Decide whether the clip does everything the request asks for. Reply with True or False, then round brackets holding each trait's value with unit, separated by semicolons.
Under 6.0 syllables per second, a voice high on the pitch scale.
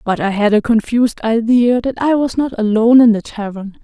True (5.4 syllables/s; 230 Hz)